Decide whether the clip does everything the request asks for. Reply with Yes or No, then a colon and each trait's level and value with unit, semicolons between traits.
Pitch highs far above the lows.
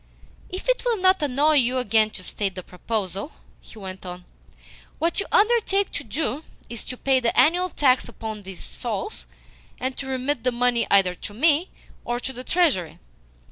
Yes: wide, 6.7 semitones